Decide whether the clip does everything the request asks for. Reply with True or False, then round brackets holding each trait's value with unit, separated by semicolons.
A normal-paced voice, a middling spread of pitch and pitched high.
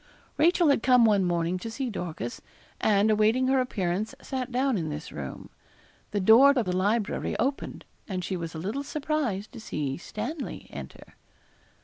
False (165 wpm; 6.2 semitones; 215 Hz)